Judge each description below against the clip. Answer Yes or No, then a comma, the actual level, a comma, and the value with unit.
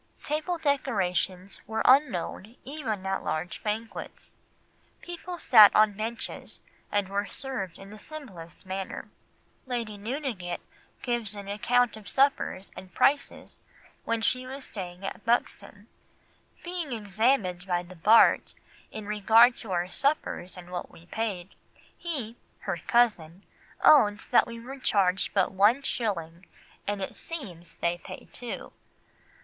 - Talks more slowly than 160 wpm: Yes, slow, 135 wpm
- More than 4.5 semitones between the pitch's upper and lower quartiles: Yes, average, 4.9 semitones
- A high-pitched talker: Yes, high, 210 Hz